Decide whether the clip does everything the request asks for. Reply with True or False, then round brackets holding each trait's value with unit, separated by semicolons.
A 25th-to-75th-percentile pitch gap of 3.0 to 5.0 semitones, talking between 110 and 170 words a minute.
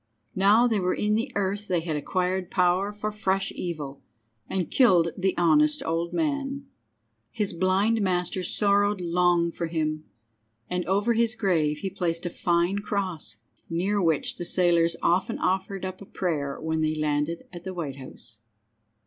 True (3.3 semitones; 160 wpm)